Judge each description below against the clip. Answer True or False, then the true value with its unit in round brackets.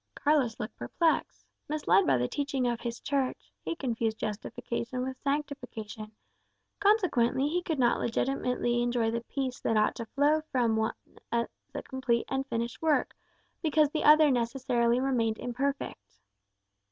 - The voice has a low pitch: False (250 Hz)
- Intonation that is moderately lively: True (3.5 semitones)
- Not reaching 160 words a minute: True (150 wpm)